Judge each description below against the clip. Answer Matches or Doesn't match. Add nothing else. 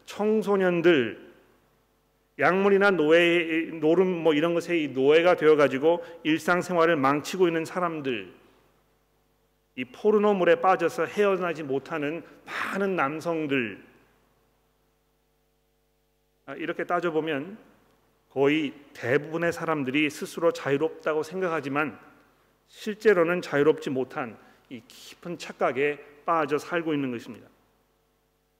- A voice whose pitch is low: Doesn't match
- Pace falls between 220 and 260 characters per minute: Matches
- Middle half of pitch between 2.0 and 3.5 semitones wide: Matches